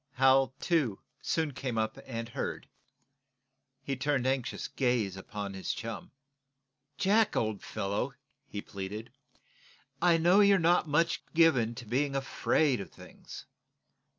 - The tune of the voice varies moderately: No, wide, 6.2 semitones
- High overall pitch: No, low, 130 Hz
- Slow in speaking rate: Yes, slow, 125 wpm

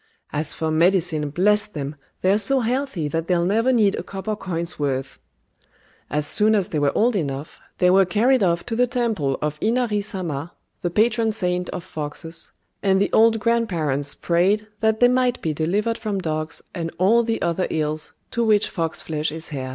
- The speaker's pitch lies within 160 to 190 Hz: Yes, medium, 185 Hz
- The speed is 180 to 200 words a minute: Yes, average, 190 wpm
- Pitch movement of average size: No, wide, 5.7 semitones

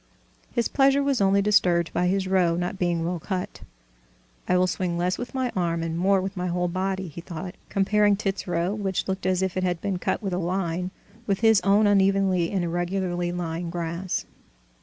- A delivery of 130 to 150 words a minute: No, average, 200 wpm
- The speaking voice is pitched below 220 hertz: Yes, medium, 185 Hz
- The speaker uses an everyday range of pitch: No, narrow, 2.0 semitones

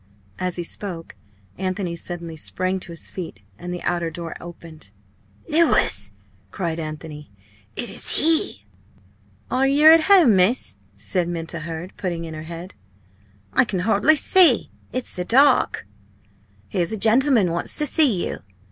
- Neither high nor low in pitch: Yes, medium, 180 Hz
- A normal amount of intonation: No, wide, 6.5 semitones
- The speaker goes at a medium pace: Yes, average, 150 wpm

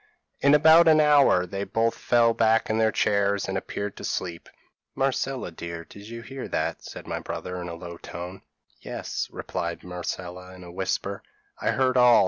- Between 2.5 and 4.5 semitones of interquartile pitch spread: No, wide, 5.4 semitones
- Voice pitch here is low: Yes, low, 100 Hz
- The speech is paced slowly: No, average, 175 wpm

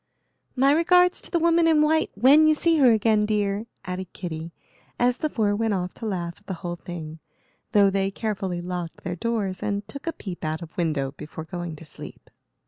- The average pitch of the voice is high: Yes, high, 200 Hz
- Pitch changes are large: Yes, wide, 6.2 semitones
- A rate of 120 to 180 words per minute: No, fast, 205 wpm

